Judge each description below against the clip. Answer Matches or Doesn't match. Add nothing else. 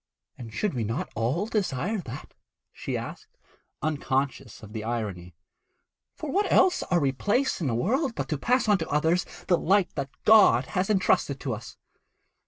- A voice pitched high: Doesn't match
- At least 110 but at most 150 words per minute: Doesn't match